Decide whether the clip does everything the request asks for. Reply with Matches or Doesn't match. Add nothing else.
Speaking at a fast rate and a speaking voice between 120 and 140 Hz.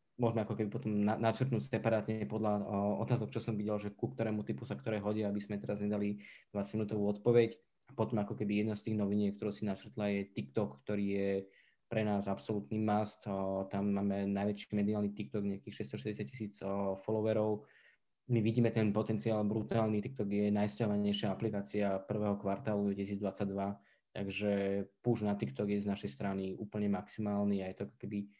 Doesn't match